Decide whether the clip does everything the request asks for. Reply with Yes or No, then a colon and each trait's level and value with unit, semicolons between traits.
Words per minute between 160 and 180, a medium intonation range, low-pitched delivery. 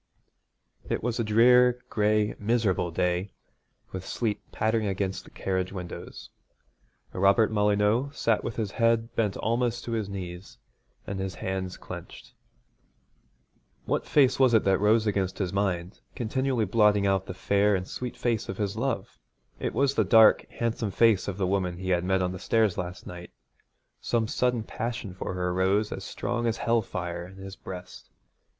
Yes: average, 165 wpm; average, 3.5 semitones; low, 105 Hz